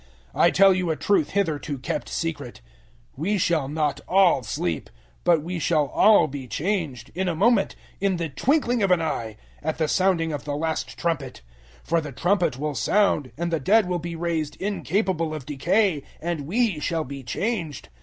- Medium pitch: Yes, medium, 165 Hz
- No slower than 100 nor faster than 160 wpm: No, average, 185 wpm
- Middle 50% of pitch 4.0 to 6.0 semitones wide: Yes, average, 4.4 semitones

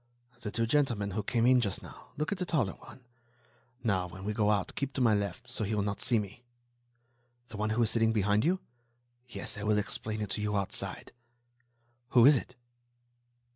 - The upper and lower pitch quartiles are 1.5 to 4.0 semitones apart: Yes, average, 3.0 semitones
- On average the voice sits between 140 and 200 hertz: No, low, 110 Hz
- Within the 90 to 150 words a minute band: No, fast, 205 wpm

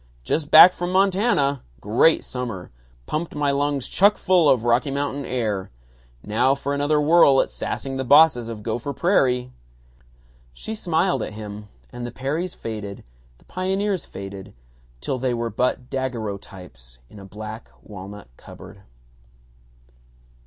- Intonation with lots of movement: Yes, wide, 6.0 semitones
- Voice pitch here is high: No, low, 130 Hz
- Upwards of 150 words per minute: No, average, 140 wpm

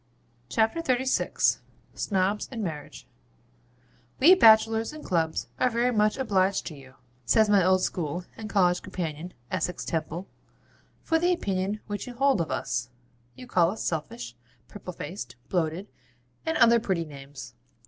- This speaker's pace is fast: No, average, 145 wpm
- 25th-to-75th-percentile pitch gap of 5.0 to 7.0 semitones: Yes, average, 5.3 semitones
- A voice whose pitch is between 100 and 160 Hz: No, high, 190 Hz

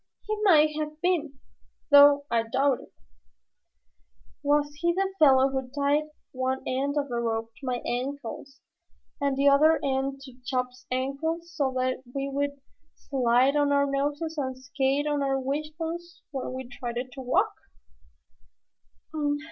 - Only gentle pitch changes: Yes, narrow, 2.3 semitones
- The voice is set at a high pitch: Yes, very high, 275 Hz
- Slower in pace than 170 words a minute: Yes, average, 145 wpm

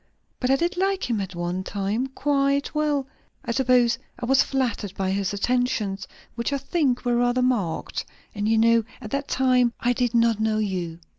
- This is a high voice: Yes, high, 240 Hz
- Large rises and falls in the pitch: No, average, 4.4 semitones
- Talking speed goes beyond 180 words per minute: Yes, average, 190 wpm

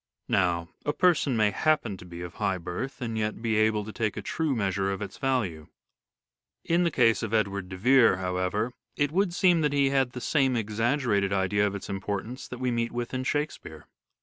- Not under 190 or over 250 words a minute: Yes, fast, 205 wpm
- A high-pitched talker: No, low, 110 Hz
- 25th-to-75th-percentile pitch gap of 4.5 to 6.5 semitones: Yes, wide, 5.4 semitones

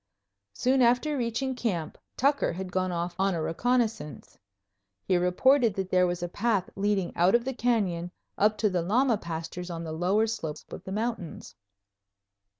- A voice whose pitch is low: No, high, 195 Hz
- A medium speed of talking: Yes, average, 165 wpm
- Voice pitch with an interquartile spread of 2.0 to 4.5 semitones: No, average, 5.1 semitones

